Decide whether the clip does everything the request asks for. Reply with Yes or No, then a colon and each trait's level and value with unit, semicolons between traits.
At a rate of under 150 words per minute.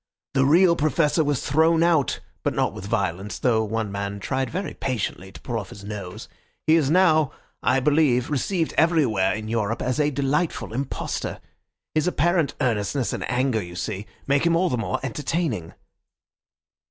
No: average, 165 wpm